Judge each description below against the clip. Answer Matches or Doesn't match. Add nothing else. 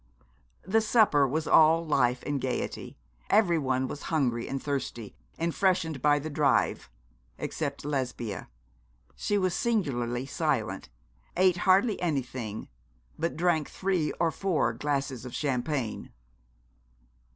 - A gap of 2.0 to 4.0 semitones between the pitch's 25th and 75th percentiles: Doesn't match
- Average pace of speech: Doesn't match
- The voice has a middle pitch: Matches